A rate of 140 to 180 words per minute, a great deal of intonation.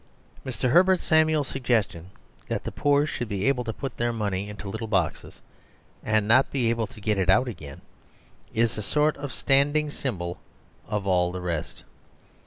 Yes: average, 175 wpm; wide, 5.7 semitones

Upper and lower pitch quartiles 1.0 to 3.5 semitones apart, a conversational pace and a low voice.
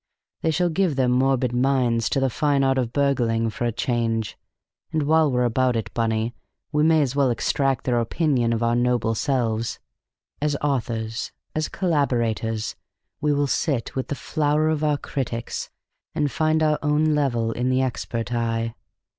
No: average, 4.1 semitones; average, 170 wpm; low, 130 Hz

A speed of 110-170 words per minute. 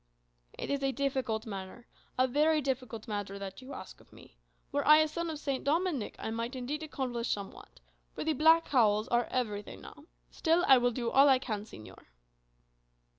No: average, 185 wpm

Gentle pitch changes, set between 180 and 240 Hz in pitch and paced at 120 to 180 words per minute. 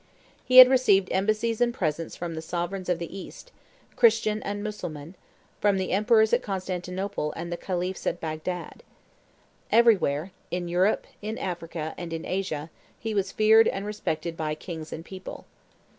No: average, 4.0 semitones; medium, 185 Hz; average, 160 wpm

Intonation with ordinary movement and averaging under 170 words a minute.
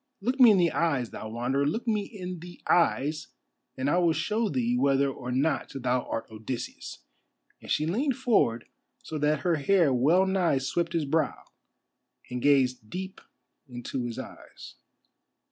No: wide, 6.1 semitones; average, 160 wpm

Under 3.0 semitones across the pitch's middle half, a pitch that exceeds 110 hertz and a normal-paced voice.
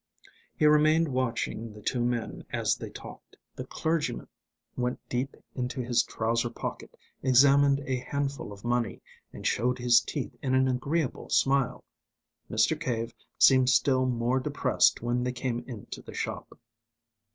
Yes: narrow, 2.5 semitones; low, 125 Hz; average, 145 wpm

